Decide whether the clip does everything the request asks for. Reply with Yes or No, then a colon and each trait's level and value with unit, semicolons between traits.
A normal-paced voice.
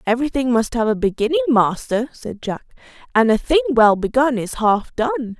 Yes: average, 180 wpm